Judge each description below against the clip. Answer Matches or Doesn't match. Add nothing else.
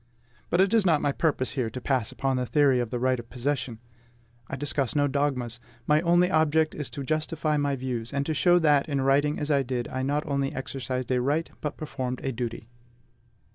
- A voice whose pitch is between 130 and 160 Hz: Matches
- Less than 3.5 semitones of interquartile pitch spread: Matches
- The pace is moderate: Doesn't match